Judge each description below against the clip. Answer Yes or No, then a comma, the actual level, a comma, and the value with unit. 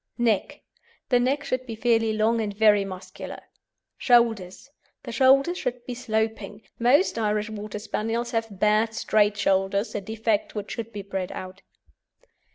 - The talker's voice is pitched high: Yes, high, 220 Hz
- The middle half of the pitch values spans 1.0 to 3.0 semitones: Yes, narrow, 2.4 semitones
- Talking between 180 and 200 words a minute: No, average, 150 wpm